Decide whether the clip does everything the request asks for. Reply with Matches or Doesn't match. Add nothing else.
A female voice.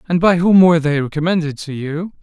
Doesn't match